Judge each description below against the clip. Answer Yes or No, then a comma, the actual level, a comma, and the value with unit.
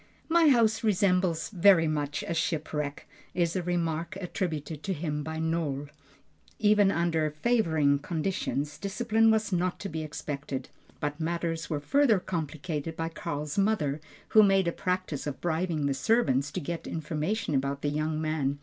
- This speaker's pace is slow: No, average, 155 wpm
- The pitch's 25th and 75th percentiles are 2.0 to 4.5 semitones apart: Yes, average, 4.1 semitones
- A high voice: No, medium, 165 Hz